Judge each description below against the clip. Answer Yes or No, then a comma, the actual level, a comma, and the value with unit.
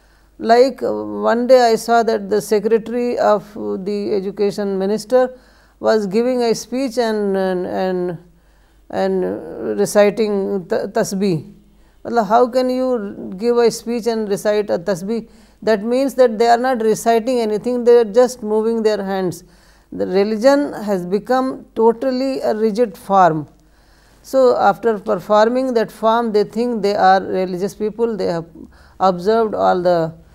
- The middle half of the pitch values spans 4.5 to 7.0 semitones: No, average, 3.2 semitones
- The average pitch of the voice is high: Yes, high, 215 Hz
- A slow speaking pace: No, average, 135 wpm